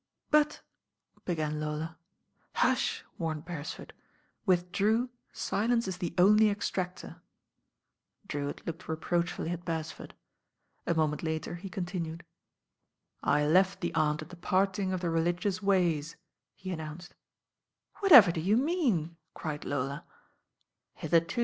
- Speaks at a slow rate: Yes, slow, 125 wpm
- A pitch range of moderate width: Yes, average, 3.4 semitones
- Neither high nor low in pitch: Yes, medium, 175 Hz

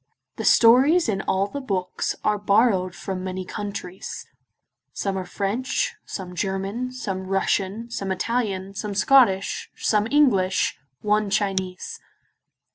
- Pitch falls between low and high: No, high, 200 Hz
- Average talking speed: No, slow, 120 wpm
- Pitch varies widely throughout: No, average, 3.2 semitones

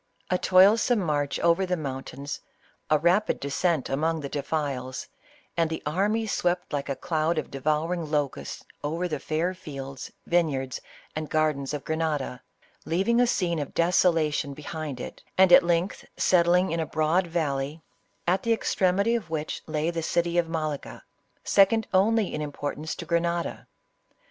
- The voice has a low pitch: No, medium, 160 Hz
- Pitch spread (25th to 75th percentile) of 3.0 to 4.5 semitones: Yes, average, 3.4 semitones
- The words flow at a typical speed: Yes, average, 160 wpm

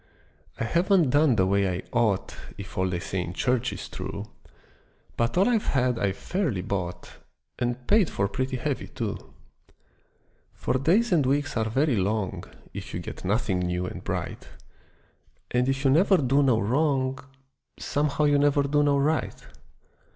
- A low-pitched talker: Yes, low, 130 Hz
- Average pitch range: No, wide, 6.4 semitones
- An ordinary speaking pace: Yes, average, 165 wpm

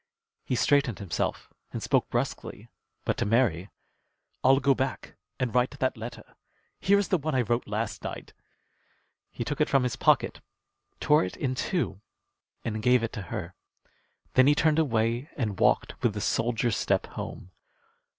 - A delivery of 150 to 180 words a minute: Yes, average, 165 wpm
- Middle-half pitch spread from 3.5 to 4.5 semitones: Yes, average, 3.8 semitones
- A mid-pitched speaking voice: No, low, 125 Hz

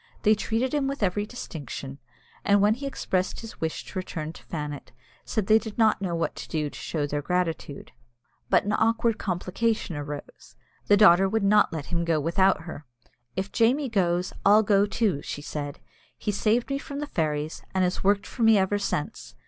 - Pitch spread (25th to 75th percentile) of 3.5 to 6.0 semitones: Yes, average, 5.2 semitones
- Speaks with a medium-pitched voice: No, high, 195 Hz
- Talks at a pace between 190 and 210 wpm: Yes, average, 195 wpm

